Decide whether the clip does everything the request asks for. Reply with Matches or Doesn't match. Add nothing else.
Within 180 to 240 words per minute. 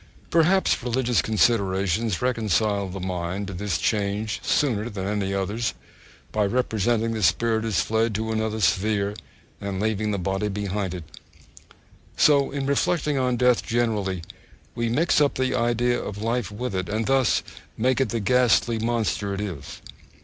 Doesn't match